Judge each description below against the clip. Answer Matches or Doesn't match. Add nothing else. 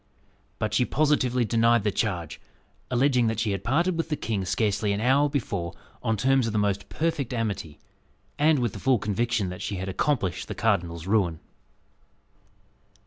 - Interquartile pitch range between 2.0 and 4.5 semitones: Doesn't match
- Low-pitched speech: Matches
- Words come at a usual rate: Matches